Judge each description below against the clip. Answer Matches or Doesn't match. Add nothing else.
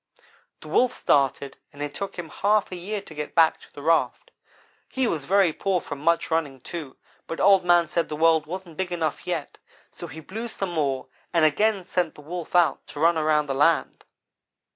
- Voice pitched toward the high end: Doesn't match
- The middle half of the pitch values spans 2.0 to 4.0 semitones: Matches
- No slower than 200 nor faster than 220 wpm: Matches